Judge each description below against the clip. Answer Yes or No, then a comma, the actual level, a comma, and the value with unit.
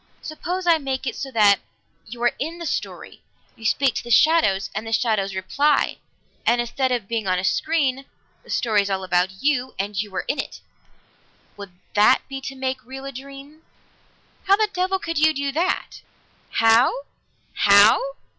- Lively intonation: Yes, wide, 5.7 semitones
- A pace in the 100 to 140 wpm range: No, average, 180 wpm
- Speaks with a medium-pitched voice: No, very high, 260 Hz